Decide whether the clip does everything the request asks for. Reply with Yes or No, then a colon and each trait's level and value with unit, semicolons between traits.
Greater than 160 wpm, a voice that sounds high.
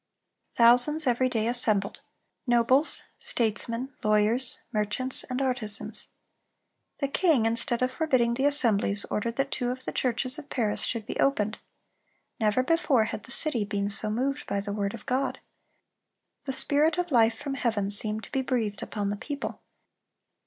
No: average, 155 wpm; high, 240 Hz